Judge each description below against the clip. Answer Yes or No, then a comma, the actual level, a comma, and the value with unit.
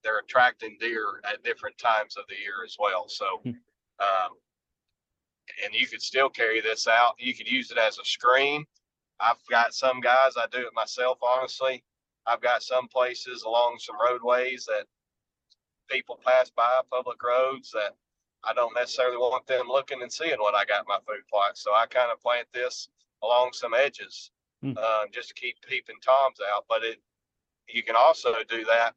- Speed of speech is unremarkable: Yes, average, 180 wpm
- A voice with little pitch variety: Yes, narrow, 1.7 semitones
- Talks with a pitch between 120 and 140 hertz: Yes, low, 125 Hz